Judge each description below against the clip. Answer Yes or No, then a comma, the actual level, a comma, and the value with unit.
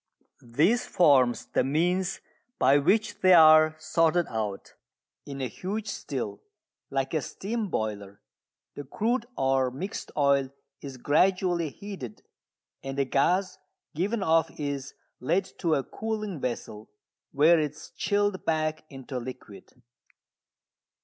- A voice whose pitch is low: No, medium, 155 Hz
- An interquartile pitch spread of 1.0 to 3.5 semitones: No, wide, 5.6 semitones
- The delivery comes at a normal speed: No, slow, 125 wpm